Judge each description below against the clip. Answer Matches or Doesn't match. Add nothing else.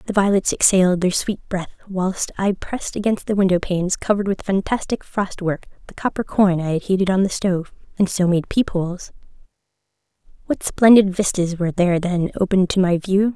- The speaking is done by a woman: Matches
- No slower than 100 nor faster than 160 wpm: Doesn't match